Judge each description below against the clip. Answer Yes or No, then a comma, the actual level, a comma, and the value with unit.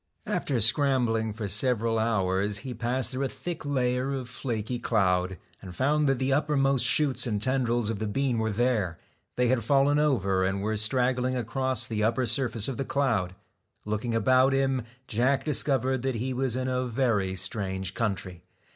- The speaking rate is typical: Yes, average, 175 wpm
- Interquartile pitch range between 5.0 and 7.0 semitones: No, average, 3.7 semitones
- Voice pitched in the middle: No, low, 120 Hz